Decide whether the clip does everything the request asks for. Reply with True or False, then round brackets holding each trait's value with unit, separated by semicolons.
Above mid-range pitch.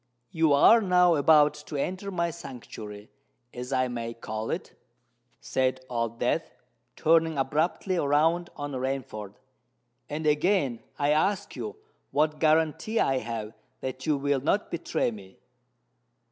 False (145 Hz)